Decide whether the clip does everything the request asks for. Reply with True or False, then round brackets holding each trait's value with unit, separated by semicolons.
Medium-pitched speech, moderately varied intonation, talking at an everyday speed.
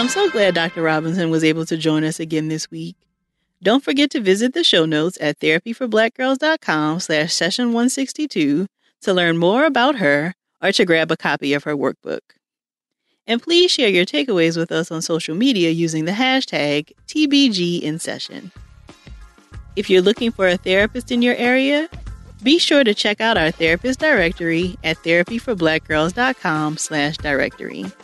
False (175 Hz; 7.4 semitones; 160 wpm)